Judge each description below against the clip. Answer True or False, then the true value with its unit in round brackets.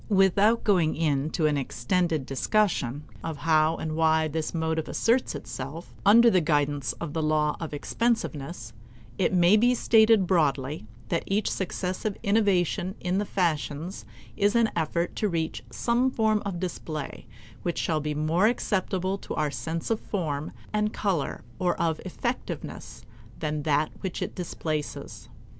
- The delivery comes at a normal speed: True (150 wpm)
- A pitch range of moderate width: True (4.6 semitones)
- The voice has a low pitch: False (170 Hz)